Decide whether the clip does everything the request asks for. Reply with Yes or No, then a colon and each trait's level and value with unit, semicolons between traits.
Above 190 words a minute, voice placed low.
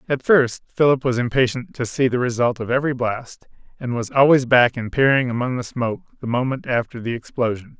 Yes: average, 200 wpm; low, 125 Hz